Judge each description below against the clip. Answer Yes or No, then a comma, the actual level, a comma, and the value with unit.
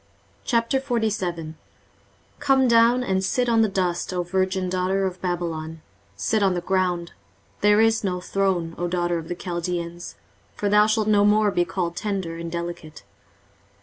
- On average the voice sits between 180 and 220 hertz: Yes, medium, 185 Hz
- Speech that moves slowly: No, average, 155 wpm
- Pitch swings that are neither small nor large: Yes, average, 3.4 semitones